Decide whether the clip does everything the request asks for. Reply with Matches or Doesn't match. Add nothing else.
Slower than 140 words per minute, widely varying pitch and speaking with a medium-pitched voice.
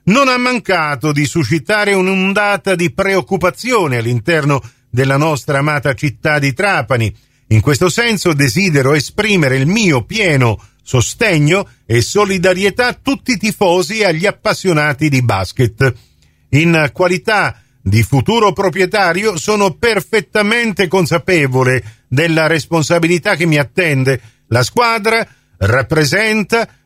Matches